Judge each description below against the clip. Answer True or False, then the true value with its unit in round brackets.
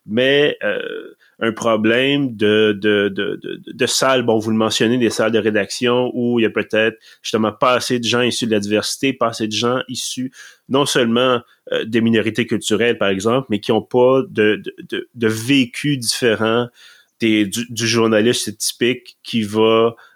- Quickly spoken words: False (185 wpm)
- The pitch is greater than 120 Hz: False (115 Hz)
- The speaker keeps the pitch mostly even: True (2.3 semitones)